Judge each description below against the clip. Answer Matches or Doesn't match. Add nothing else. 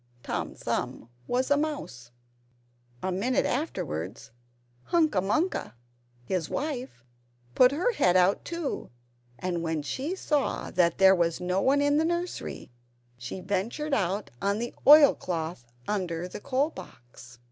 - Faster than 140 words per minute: Doesn't match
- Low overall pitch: Doesn't match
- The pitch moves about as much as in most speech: Doesn't match